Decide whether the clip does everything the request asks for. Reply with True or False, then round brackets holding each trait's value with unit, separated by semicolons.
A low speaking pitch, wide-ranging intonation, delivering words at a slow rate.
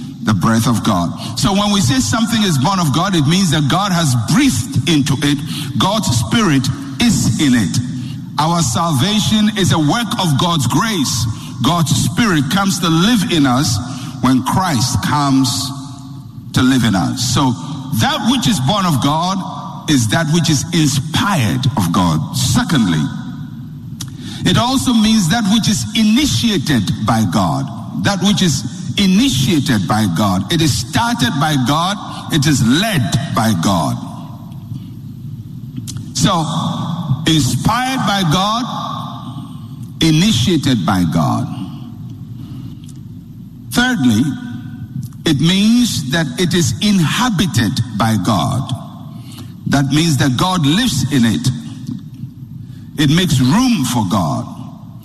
False (145 Hz; 6.0 semitones; 125 wpm)